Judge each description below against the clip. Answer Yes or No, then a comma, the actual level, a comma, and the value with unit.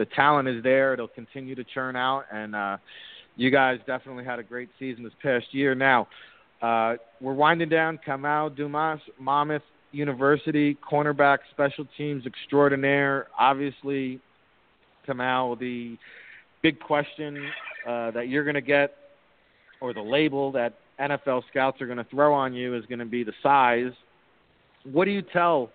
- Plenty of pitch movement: No, average, 2.8 semitones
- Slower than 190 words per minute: Yes, average, 155 wpm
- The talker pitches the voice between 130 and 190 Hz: Yes, low, 135 Hz